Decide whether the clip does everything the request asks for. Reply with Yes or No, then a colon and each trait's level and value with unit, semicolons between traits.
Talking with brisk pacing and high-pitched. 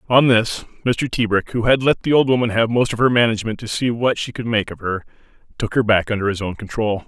No: fast, 255 wpm; low, 115 Hz